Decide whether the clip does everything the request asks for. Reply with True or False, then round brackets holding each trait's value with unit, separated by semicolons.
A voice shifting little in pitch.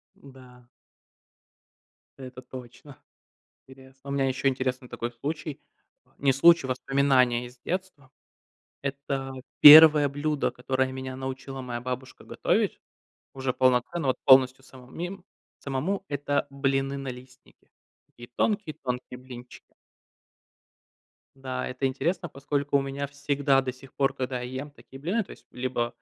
True (1.7 semitones)